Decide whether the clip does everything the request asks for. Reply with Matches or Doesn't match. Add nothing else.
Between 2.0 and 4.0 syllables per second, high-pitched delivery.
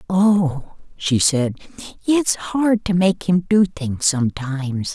Doesn't match